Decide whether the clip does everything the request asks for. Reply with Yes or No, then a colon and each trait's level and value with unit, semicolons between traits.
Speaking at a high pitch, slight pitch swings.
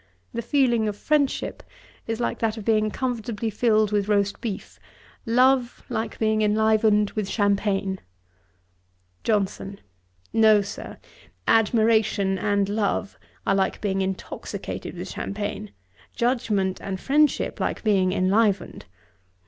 Yes: high, 215 Hz; narrow, 2.2 semitones